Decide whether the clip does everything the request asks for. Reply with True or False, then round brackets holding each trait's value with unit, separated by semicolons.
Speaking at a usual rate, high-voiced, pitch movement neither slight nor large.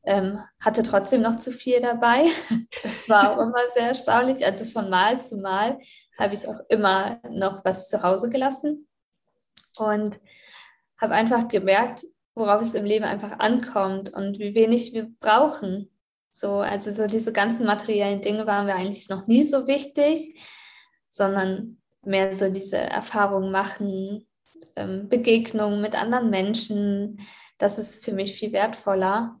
True (145 wpm; 215 Hz; 3.1 semitones)